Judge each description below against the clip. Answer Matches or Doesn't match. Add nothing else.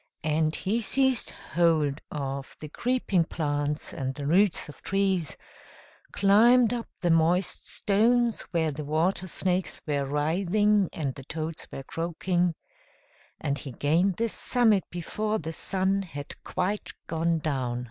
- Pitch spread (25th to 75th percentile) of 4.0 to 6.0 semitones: Matches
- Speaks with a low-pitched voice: Doesn't match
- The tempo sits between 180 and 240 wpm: Doesn't match